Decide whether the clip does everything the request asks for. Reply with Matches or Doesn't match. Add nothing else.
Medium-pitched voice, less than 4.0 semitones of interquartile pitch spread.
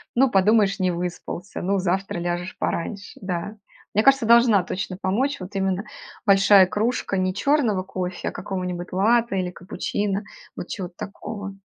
Doesn't match